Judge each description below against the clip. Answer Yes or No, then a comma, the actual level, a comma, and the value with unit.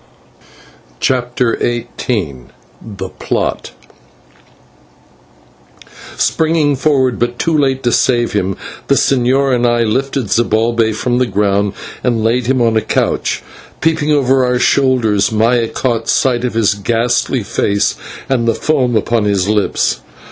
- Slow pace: Yes, slow, 130 wpm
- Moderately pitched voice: No, low, 120 Hz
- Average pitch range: Yes, average, 3.0 semitones